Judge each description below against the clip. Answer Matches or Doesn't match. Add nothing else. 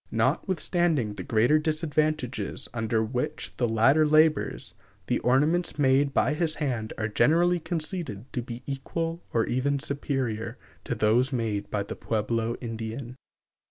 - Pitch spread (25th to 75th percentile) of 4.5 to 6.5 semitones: Matches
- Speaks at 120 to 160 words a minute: Matches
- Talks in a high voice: Doesn't match